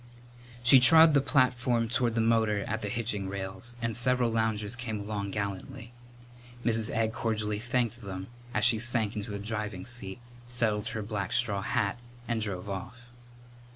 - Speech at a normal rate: Yes, average, 160 wpm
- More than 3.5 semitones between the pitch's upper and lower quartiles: No, average, 2.7 semitones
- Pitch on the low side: Yes, low, 110 Hz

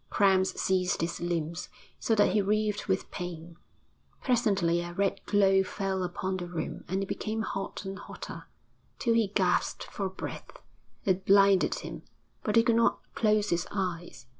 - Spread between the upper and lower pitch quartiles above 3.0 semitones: No, narrow, 2.6 semitones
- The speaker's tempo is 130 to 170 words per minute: Yes, average, 165 wpm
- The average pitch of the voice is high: Yes, high, 195 Hz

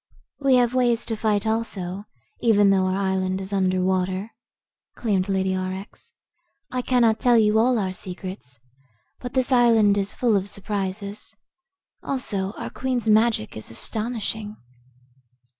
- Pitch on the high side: Yes, high, 205 Hz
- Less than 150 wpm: Yes, average, 140 wpm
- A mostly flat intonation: No, average, 3.5 semitones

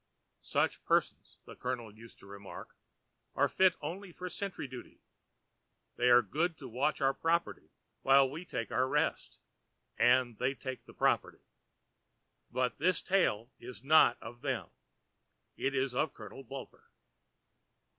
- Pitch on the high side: No, low, 130 Hz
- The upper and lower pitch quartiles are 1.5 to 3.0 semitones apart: No, average, 4.3 semitones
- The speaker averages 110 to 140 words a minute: Yes, slow, 135 wpm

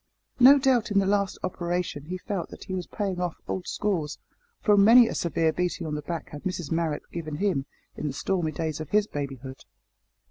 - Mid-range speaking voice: Yes, medium, 175 Hz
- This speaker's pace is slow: No, fast, 205 wpm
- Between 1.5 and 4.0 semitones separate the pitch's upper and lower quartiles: No, average, 4.4 semitones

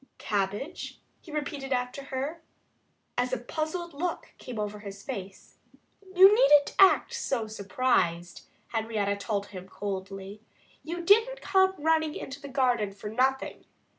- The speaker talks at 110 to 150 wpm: Yes, slow, 135 wpm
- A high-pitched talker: Yes, very high, 255 Hz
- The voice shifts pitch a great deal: Yes, wide, 7.3 semitones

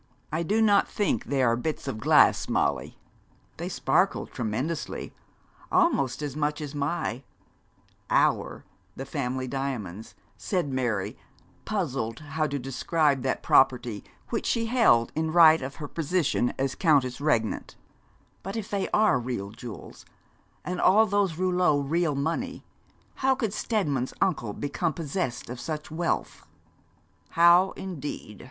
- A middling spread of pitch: No, wide, 5.8 semitones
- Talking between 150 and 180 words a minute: No, slow, 135 wpm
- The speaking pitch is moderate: Yes, medium, 150 Hz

